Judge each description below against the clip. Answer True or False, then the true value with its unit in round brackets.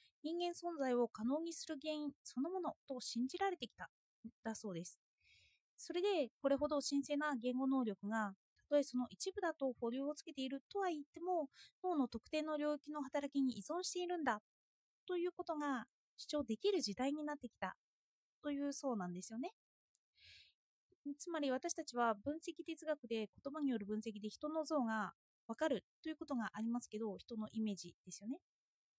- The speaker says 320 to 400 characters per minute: True (345 characters per minute)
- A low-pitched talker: False (280 Hz)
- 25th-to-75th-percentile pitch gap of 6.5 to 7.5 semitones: False (5.4 semitones)